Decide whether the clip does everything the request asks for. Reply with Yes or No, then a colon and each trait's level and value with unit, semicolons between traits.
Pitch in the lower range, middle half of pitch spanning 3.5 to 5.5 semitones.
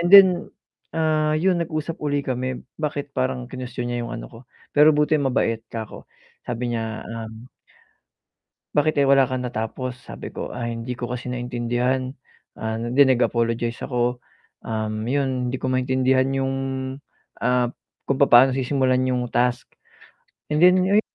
No: low, 130 Hz; average, 2.8 semitones